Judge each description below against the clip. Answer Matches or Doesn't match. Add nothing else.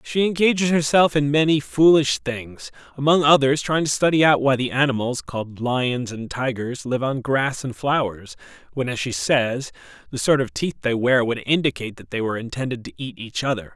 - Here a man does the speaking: Matches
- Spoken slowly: Doesn't match